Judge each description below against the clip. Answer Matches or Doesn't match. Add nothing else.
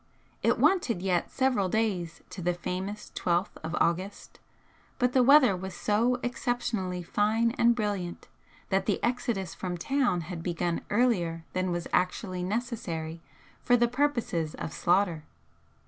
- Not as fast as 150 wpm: Matches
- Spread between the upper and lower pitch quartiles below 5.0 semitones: Doesn't match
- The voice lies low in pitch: Doesn't match